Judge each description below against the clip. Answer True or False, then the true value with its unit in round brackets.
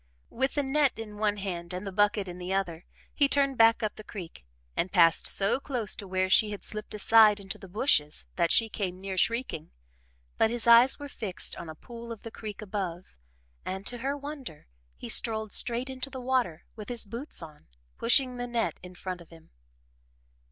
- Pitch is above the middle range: True (210 Hz)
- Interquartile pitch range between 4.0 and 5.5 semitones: True (4.5 semitones)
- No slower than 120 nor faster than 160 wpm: False (200 wpm)